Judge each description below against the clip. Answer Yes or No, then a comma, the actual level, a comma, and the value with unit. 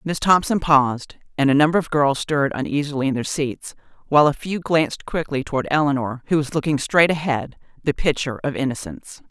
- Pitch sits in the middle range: Yes, medium, 145 Hz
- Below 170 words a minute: No, average, 185 wpm